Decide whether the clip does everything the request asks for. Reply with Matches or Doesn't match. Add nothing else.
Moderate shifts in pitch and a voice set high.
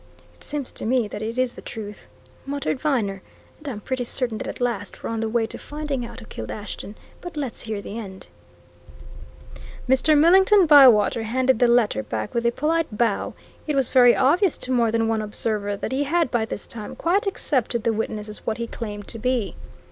Matches